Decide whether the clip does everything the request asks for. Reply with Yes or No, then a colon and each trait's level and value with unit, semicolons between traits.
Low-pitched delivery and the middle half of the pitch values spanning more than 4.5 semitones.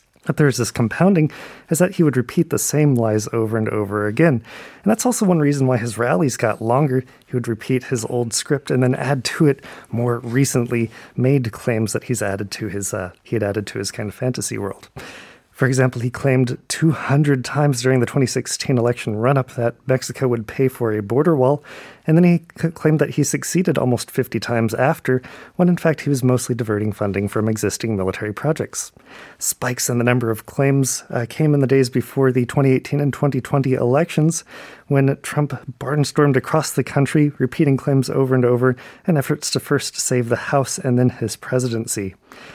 No: low, 130 Hz; average, 3.5 semitones